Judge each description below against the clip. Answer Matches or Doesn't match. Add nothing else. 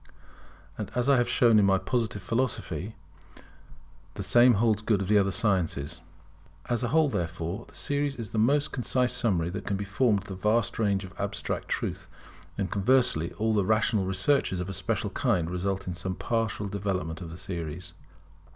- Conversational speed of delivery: Matches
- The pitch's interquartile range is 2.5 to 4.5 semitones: Matches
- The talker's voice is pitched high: Doesn't match